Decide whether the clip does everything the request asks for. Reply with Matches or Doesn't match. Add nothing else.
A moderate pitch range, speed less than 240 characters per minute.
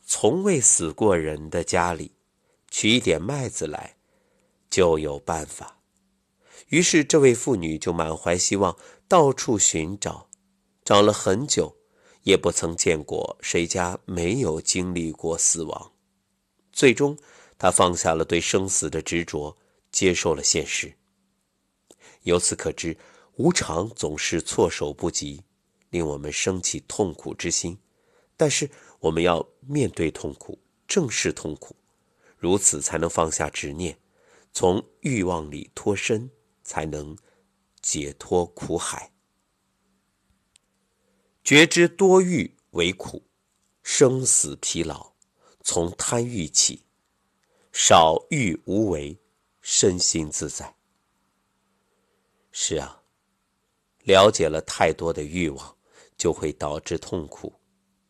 Matches